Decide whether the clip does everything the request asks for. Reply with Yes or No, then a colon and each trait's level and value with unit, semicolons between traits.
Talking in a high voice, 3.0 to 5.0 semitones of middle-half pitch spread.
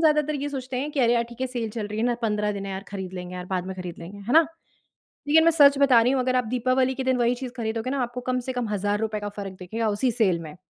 Yes: high, 235 Hz; average, 4.1 semitones